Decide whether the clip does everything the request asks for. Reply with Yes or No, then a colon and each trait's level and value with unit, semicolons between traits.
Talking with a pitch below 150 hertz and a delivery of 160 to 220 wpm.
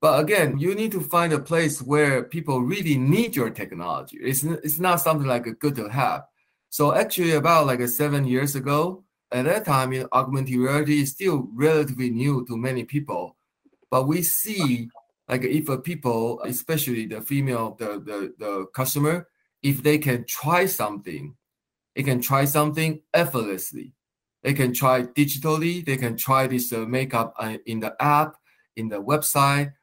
Yes: low, 135 Hz; average, 170 wpm